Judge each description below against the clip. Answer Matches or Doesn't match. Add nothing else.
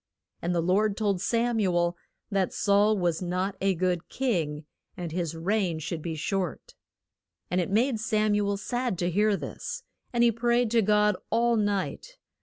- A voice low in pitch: Doesn't match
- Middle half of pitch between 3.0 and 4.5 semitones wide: Matches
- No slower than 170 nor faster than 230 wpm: Matches